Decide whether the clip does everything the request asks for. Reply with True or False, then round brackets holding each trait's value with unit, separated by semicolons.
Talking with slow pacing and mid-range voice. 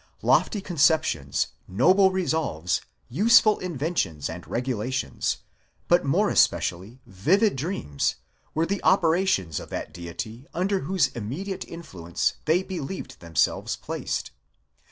True (115 wpm; 150 Hz)